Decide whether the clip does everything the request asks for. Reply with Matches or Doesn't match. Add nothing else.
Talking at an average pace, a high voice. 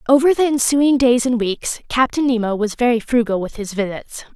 Matches